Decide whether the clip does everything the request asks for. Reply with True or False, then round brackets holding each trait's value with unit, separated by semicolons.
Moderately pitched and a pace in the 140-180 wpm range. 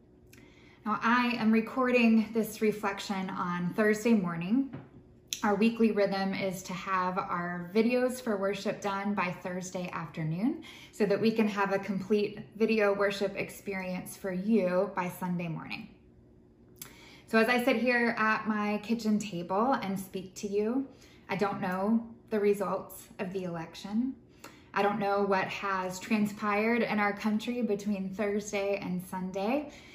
False (200 Hz; 145 wpm)